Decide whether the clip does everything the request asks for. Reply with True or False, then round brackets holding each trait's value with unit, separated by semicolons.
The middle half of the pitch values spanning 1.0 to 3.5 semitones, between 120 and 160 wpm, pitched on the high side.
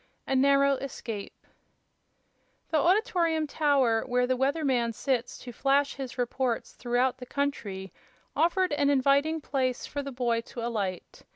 True (2.9 semitones; 145 wpm; 265 Hz)